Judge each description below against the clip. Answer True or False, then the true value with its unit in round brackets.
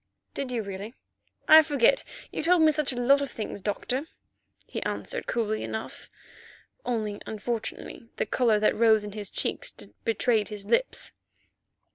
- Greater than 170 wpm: False (150 wpm)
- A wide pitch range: False (4.5 semitones)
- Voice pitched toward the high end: True (230 Hz)